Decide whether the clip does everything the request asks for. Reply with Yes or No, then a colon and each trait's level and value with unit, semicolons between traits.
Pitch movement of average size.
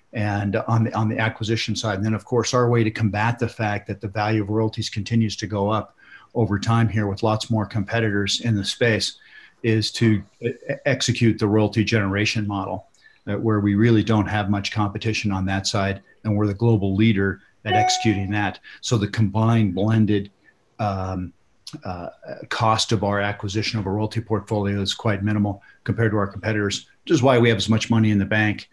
No: narrow, 1.6 semitones